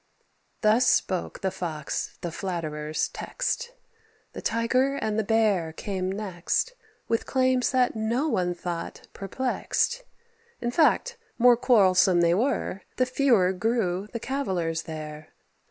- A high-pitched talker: Yes, high, 210 Hz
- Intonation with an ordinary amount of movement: No, wide, 6.0 semitones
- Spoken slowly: Yes, slow, 125 wpm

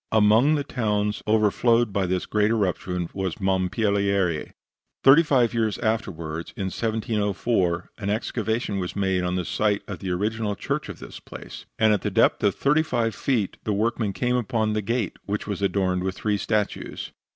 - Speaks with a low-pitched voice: Yes, low, 105 Hz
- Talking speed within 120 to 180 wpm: Yes, average, 175 wpm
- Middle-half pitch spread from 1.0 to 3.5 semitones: Yes, average, 2.9 semitones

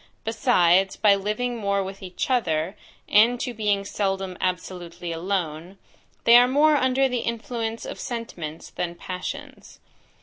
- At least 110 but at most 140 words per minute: Yes, slow, 135 wpm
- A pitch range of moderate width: Yes, average, 4.8 semitones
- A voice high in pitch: Yes, high, 200 Hz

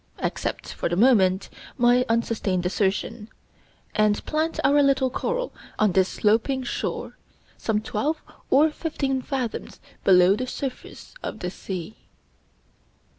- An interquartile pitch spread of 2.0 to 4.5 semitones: No, average, 5.2 semitones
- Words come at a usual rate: No, slow, 125 wpm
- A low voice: No, high, 230 Hz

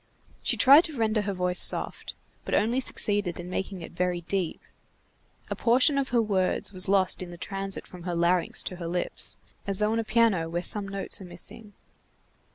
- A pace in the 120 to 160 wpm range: No, average, 195 wpm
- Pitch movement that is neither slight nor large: Yes, average, 3.3 semitones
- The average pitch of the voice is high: Yes, high, 195 Hz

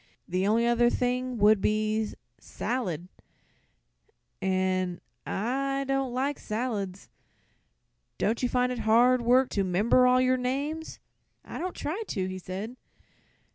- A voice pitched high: Yes, high, 235 Hz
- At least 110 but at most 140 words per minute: Yes, slow, 135 wpm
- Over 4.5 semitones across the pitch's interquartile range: No, average, 4.2 semitones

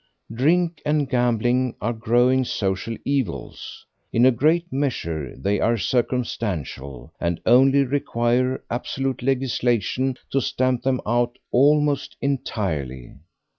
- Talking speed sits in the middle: No, slow, 110 wpm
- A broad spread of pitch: No, average, 3.3 semitones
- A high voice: No, low, 125 Hz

